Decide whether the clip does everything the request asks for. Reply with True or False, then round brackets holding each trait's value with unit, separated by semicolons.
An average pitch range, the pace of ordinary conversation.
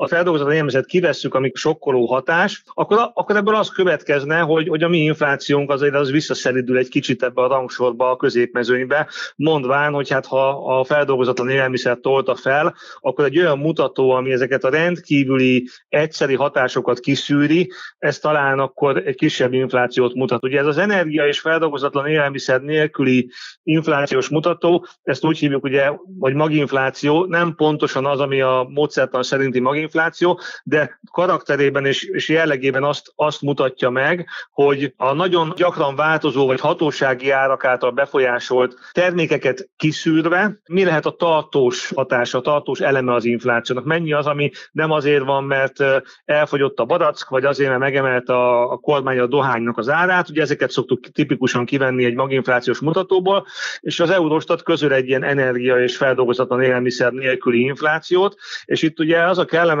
False (3.4 semitones; 160 wpm)